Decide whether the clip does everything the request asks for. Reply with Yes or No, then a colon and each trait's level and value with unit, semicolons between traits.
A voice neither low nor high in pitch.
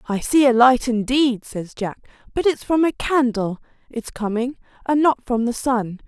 No: high, 245 Hz